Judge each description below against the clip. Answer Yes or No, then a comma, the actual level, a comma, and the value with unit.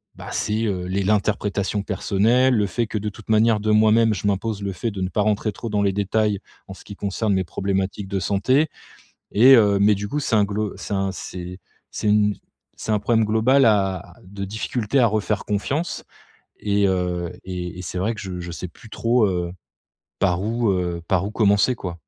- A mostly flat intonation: Yes, narrow, 2.3 semitones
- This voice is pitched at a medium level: No, low, 105 Hz